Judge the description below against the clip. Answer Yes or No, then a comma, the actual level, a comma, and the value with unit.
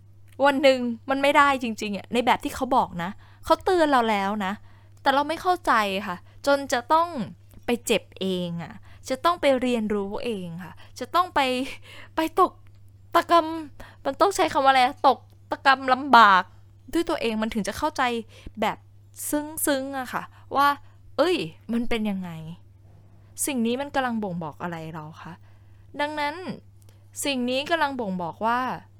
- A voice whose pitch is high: Yes, high, 235 Hz